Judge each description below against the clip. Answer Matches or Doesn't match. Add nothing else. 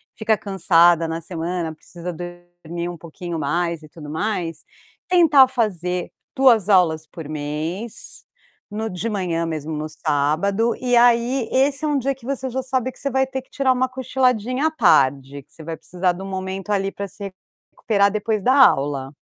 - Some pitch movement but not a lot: Doesn't match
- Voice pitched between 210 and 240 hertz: Doesn't match